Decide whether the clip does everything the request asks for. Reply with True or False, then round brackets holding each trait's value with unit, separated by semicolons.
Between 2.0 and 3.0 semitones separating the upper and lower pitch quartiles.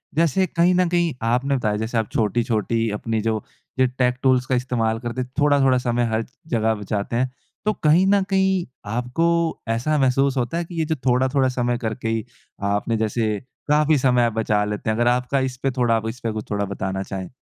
False (4.0 semitones)